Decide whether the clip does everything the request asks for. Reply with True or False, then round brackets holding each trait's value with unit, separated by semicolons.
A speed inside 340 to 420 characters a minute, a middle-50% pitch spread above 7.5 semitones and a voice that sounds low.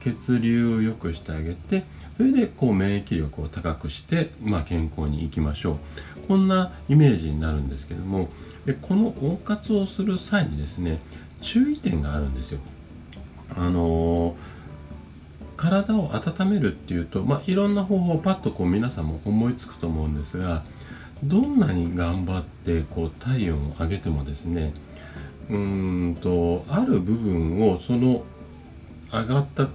False (300 characters per minute; 8.7 semitones; 85 Hz)